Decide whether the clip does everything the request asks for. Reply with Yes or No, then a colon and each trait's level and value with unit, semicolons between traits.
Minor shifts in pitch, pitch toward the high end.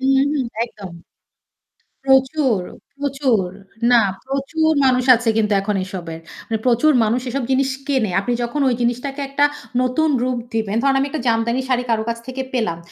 No: average, 3.3 semitones; very high, 250 Hz